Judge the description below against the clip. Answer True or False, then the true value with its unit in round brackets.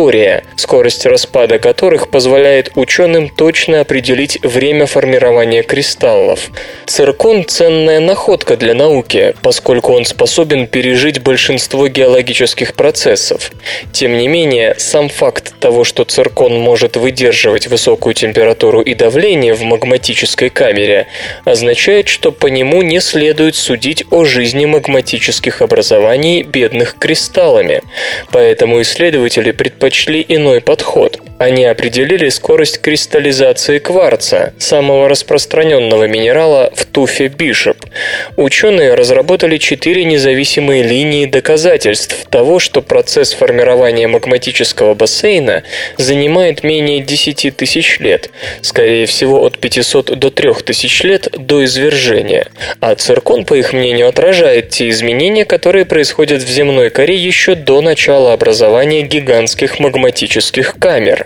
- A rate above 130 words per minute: False (115 wpm)